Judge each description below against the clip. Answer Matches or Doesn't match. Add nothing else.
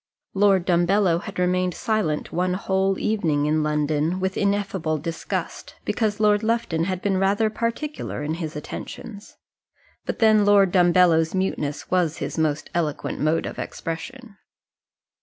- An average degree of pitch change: Matches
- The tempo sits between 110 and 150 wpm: Matches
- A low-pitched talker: Doesn't match